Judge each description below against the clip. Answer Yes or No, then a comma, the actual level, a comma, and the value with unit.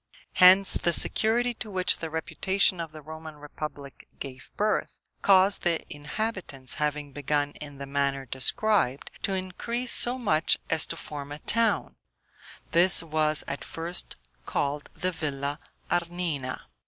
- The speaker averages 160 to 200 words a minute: No, average, 140 wpm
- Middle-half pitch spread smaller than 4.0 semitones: No, average, 4.6 semitones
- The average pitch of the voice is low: No, medium, 160 Hz